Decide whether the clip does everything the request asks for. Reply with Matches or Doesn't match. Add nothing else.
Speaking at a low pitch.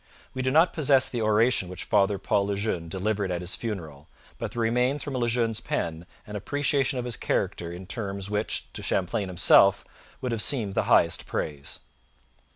Matches